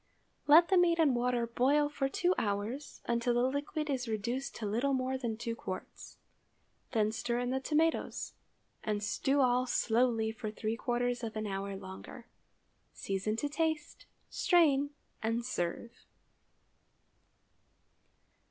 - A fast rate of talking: No, slow, 135 wpm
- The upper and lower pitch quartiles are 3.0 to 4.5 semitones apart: Yes, average, 4.1 semitones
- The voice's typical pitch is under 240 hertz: No, high, 245 Hz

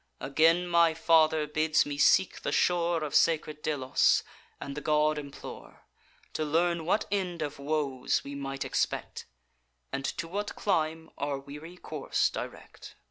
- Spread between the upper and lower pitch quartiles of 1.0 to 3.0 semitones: Yes, narrow, 2.6 semitones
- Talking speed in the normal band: Yes, average, 145 wpm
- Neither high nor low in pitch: Yes, medium, 155 Hz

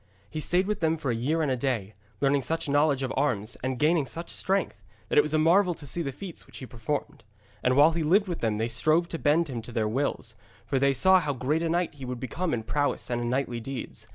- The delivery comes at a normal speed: No, fast, 255 wpm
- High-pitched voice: No, medium, 145 Hz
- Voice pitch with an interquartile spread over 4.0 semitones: Yes, average, 4.6 semitones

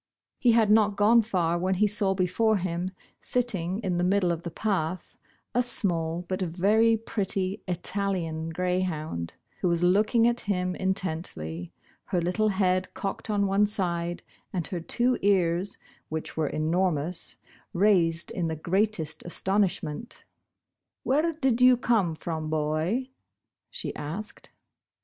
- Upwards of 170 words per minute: No, average, 140 wpm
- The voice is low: No, medium, 185 Hz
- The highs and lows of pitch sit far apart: No, average, 3.8 semitones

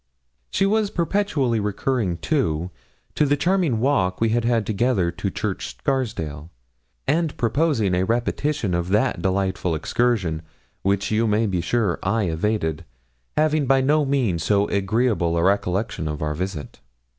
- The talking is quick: No, average, 145 wpm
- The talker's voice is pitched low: Yes, low, 110 Hz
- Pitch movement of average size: No, wide, 6.5 semitones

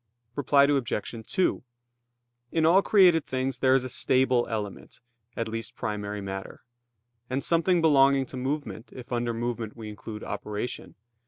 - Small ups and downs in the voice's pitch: No, average, 4.0 semitones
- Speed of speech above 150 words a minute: No, average, 145 wpm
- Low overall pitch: Yes, low, 125 Hz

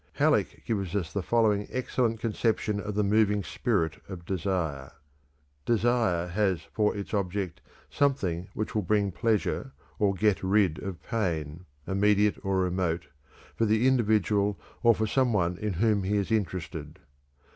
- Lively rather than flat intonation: No, average, 3.1 semitones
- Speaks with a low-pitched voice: Yes, low, 100 Hz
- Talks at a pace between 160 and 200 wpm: No, average, 145 wpm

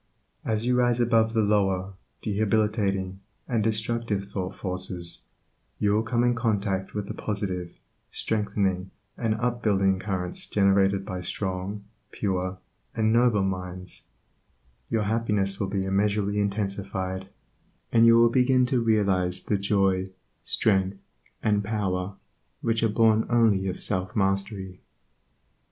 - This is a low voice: Yes, low, 100 Hz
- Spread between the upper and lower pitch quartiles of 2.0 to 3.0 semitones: Yes, average, 2.7 semitones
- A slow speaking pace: Yes, slow, 130 wpm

